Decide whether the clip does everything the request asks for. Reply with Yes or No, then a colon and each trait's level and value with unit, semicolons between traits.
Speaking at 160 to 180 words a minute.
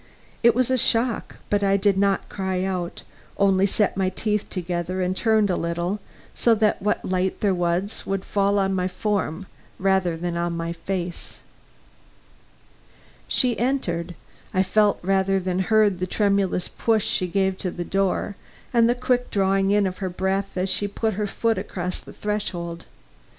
Yes: average, 170 wpm